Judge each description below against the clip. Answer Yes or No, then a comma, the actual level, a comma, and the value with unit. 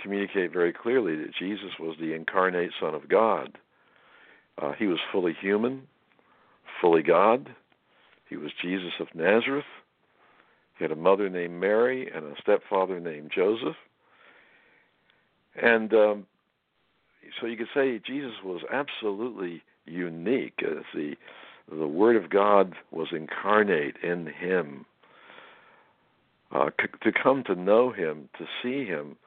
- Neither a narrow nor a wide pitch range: No, wide, 8.3 semitones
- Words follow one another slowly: Yes, slow, 130 wpm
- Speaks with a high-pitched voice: No, low, 110 Hz